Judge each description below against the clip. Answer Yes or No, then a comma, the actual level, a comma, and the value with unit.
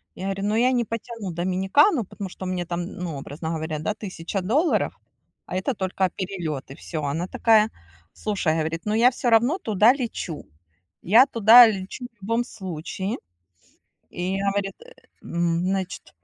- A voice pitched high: Yes, high, 195 Hz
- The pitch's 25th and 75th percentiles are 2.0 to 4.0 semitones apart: No, average, 4.5 semitones